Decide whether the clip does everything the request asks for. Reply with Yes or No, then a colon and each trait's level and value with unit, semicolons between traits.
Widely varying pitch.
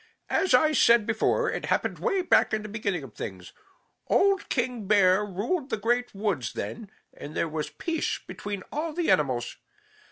Yes: wide, 7.0 semitones